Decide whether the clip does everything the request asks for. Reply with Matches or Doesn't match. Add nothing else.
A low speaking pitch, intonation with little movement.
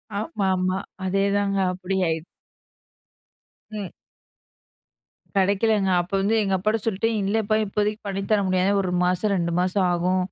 Doesn't match